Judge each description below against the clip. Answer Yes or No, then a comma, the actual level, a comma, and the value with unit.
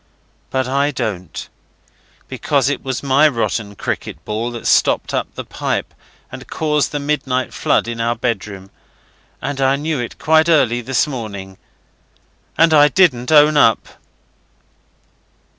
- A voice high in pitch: No, low, 130 Hz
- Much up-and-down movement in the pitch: No, average, 4.1 semitones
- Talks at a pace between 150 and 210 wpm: No, average, 140 wpm